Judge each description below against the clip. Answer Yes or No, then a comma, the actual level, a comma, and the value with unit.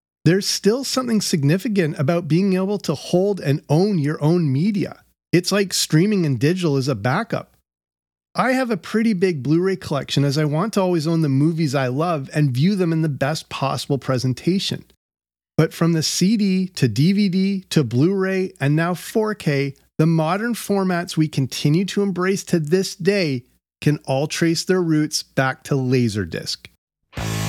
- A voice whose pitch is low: No, medium, 165 Hz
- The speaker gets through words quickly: No, average, 170 wpm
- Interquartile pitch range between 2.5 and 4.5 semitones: No, average, 5.1 semitones